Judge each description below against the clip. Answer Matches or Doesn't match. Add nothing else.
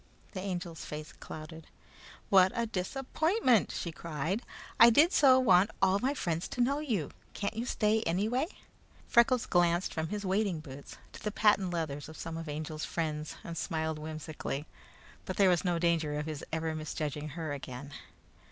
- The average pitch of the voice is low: Doesn't match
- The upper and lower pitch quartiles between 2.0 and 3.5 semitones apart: Doesn't match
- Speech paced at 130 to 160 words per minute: Doesn't match